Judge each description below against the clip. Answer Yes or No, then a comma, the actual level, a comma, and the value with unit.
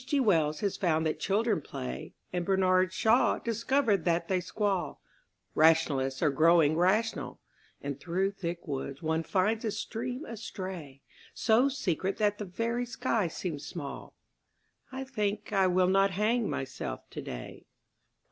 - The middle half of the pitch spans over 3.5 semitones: Yes, average, 5.2 semitones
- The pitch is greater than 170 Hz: Yes, medium, 185 Hz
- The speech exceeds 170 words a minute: No, average, 140 wpm